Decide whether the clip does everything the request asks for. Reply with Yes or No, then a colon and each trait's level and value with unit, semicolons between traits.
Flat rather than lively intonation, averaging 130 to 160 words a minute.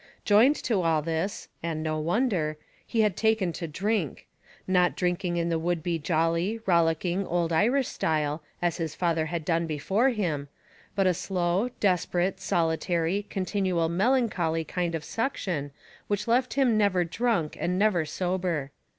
No: average, 3.8 semitones; average, 150 wpm